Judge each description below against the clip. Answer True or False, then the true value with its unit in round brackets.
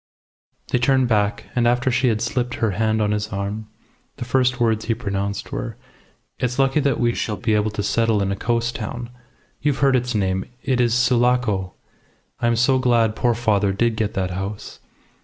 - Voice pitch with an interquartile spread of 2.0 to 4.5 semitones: True (2.9 semitones)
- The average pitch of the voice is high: False (115 Hz)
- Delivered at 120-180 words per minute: False (195 wpm)